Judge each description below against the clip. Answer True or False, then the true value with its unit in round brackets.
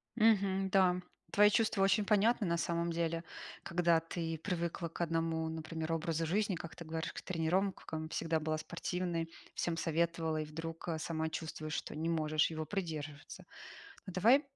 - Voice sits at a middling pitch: True (165 Hz)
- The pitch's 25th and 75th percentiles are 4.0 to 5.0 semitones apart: False (2.4 semitones)